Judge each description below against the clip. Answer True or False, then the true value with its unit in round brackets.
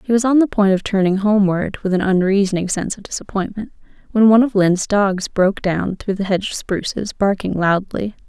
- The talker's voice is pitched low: False (200 Hz)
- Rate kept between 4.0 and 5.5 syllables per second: False (5.9 syllables/s)